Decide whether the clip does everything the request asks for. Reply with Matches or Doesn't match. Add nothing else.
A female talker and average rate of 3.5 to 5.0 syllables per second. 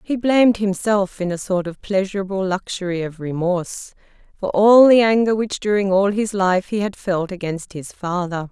Matches